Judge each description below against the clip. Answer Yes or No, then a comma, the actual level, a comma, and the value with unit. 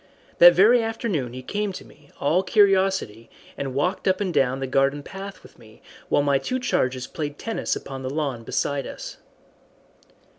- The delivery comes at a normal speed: Yes, average, 175 wpm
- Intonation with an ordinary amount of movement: No, wide, 6.4 semitones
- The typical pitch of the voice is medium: Yes, medium, 145 Hz